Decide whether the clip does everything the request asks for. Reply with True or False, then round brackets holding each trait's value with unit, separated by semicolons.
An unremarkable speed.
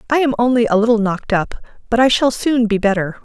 False (240 wpm)